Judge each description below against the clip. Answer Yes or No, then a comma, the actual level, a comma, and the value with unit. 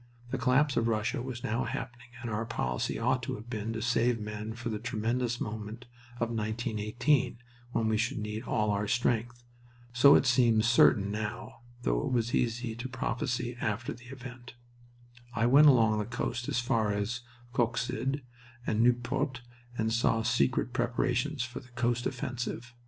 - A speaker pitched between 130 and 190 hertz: No, low, 120 Hz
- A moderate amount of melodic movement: No, narrow, 2.0 semitones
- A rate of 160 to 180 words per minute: Yes, average, 165 wpm